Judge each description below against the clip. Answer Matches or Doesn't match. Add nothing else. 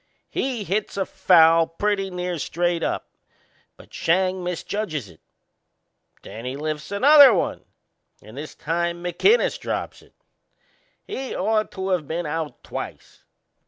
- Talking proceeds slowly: Matches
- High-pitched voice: Doesn't match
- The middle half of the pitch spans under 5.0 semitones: Matches